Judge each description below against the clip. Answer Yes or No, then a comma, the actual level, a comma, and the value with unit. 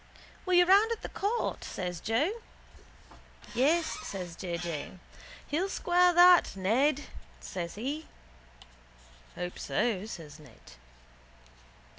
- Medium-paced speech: No, slow, 110 wpm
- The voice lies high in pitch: Yes, very high, 255 Hz